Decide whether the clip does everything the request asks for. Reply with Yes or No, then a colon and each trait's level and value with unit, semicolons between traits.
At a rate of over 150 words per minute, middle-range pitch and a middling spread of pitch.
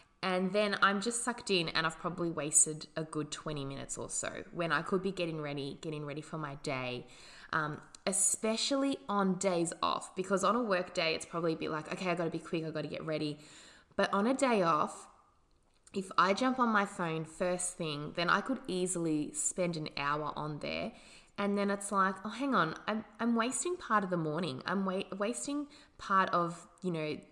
Yes: fast, 205 wpm; medium, 180 Hz; average, 4.3 semitones